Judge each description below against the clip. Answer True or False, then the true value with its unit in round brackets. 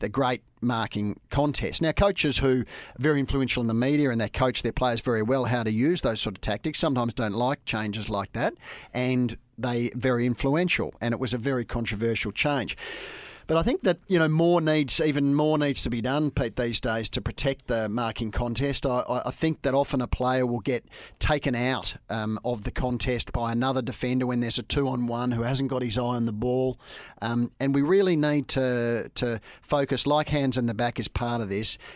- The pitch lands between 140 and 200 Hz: False (125 Hz)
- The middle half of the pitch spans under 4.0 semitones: True (3.0 semitones)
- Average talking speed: False (210 wpm)